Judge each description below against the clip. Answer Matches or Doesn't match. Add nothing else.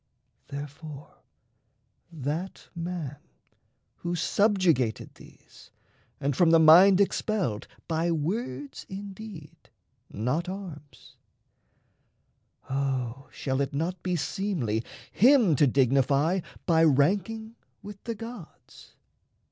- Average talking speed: Doesn't match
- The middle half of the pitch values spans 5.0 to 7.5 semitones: Matches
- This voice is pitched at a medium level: Matches